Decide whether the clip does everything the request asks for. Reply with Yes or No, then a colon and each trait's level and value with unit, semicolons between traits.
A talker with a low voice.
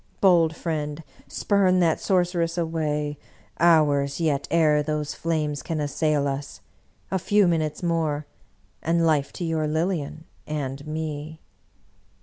No: medium, 155 Hz